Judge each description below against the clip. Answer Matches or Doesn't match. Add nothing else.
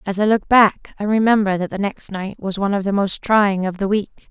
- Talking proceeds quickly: Matches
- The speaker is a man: Doesn't match